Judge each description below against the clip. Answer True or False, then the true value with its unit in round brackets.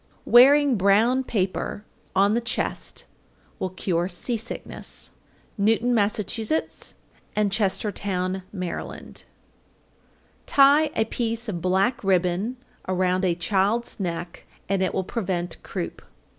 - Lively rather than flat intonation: False (3.9 semitones)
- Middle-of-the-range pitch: False (200 Hz)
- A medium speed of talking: False (120 wpm)